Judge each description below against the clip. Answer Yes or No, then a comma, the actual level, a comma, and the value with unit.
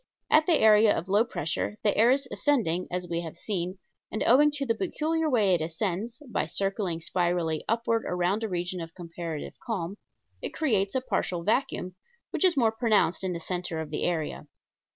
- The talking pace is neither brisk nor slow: Yes, average, 190 wpm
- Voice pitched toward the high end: Yes, high, 195 Hz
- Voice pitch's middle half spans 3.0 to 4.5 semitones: No, average, 5.0 semitones